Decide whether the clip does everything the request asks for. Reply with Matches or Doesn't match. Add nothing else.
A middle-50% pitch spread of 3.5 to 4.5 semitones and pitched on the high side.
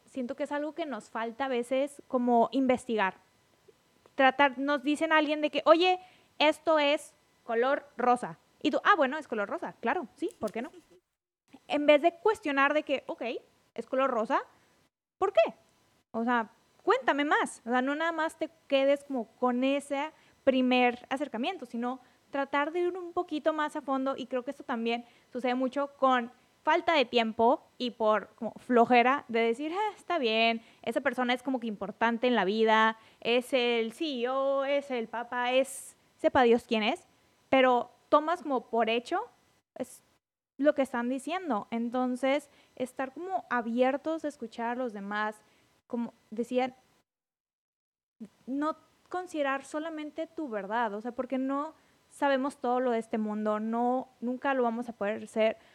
Matches